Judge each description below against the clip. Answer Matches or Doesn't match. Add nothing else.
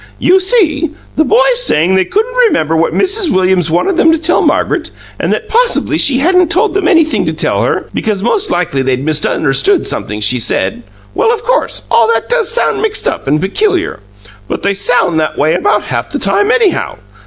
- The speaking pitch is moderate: Doesn't match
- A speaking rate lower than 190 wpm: Doesn't match